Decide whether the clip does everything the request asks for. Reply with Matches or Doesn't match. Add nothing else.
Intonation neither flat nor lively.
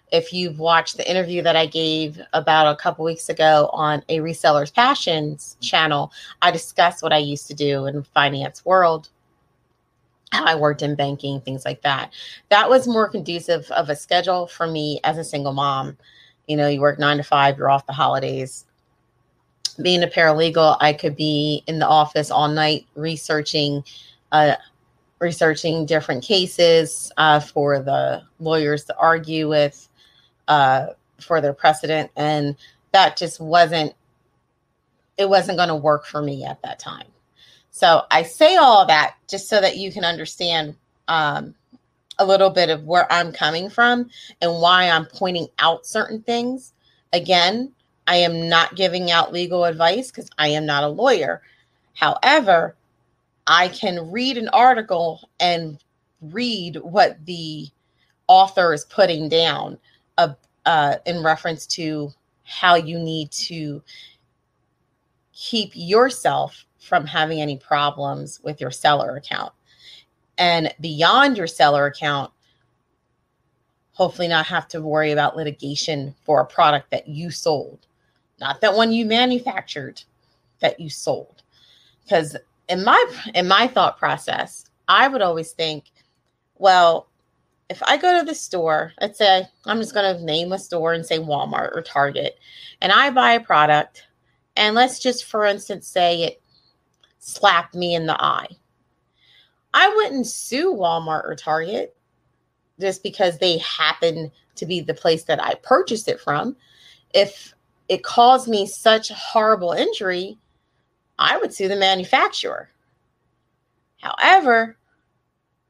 Matches